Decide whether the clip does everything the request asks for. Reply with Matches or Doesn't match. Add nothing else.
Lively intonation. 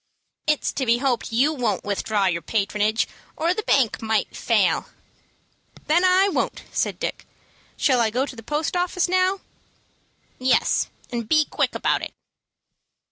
Matches